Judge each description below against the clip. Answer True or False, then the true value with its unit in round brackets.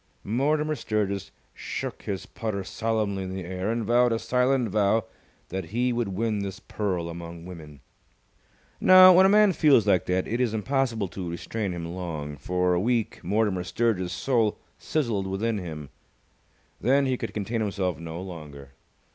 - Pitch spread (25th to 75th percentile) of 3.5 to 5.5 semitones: True (4.5 semitones)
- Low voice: True (100 Hz)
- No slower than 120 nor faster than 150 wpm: False (165 wpm)